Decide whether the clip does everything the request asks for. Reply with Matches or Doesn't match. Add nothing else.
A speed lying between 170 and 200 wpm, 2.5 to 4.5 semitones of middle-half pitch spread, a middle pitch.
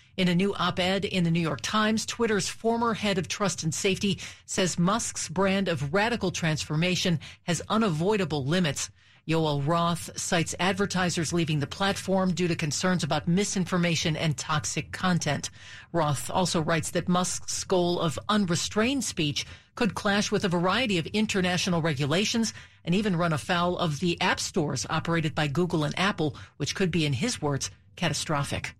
Doesn't match